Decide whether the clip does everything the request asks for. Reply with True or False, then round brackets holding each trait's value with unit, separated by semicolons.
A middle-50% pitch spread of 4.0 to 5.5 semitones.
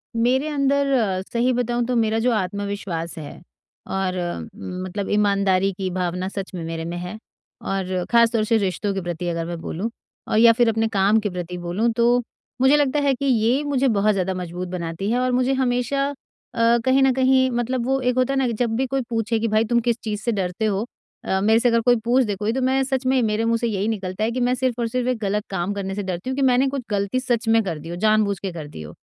True (4.5 semitones)